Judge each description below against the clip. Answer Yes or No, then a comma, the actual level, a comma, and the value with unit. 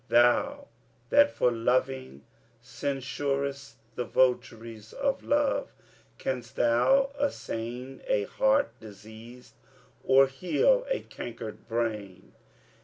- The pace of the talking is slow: Yes, slow, 95 wpm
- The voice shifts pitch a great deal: Yes, wide, 7.6 semitones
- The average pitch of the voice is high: No, low, 125 Hz